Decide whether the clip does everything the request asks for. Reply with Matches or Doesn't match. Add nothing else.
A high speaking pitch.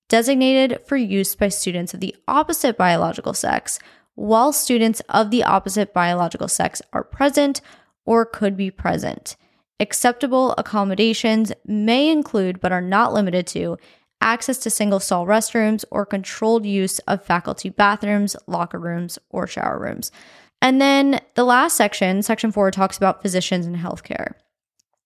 Matches